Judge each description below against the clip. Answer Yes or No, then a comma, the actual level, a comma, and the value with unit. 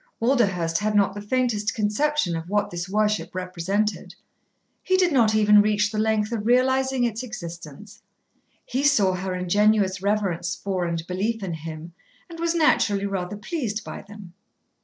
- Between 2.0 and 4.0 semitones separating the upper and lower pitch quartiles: Yes, average, 3.7 semitones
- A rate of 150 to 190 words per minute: Yes, average, 160 wpm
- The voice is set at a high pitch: Yes, high, 210 Hz